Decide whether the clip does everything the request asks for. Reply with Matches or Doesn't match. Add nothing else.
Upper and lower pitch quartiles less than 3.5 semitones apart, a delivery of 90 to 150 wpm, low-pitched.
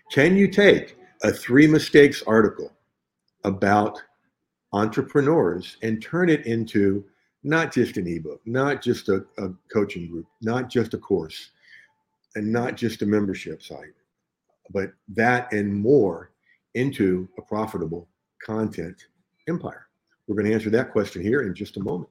Doesn't match